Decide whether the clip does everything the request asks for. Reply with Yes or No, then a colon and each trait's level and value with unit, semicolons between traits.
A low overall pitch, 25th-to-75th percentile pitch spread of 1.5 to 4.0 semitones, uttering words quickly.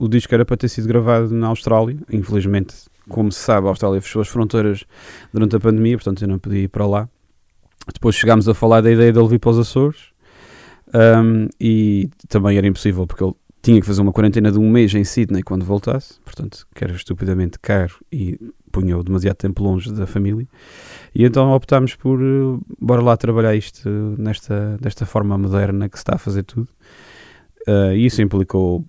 Yes: low, 105 Hz; average, 2.8 semitones; fast, 195 wpm